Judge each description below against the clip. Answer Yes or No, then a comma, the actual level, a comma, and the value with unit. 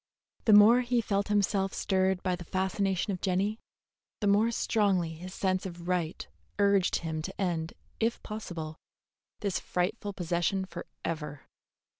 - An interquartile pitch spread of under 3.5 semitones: Yes, average, 2.8 semitones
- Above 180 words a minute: No, average, 140 wpm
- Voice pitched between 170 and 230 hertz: Yes, high, 190 Hz